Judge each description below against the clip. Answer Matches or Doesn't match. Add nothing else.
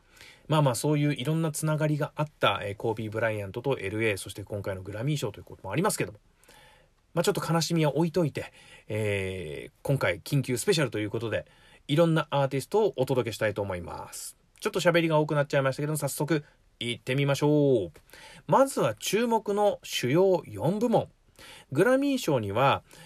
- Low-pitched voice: Doesn't match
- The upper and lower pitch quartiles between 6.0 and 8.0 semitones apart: Matches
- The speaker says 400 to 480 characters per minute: Matches